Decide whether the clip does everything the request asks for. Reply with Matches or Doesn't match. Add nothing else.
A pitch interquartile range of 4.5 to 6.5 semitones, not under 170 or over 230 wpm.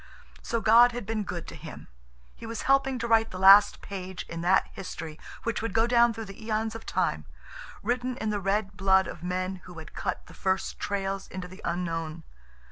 Doesn't match